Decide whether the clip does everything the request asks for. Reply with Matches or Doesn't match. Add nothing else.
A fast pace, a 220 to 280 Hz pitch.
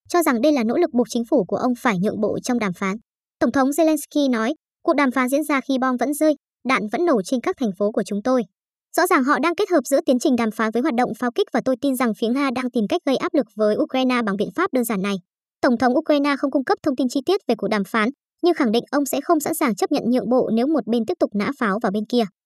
Matches